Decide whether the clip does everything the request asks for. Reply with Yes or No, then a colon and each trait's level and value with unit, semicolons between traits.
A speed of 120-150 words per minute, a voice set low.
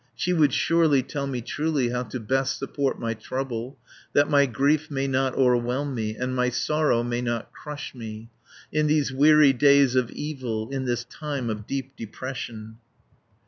No: average, 170 wpm; low, 130 Hz